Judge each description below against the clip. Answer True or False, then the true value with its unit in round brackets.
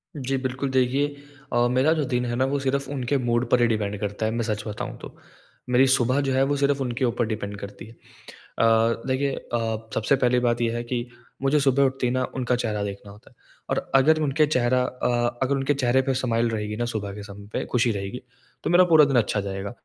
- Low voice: True (125 Hz)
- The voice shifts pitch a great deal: False (3.0 semitones)